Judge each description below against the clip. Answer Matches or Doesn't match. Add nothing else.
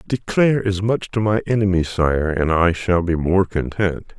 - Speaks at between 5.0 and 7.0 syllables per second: Doesn't match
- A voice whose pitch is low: Matches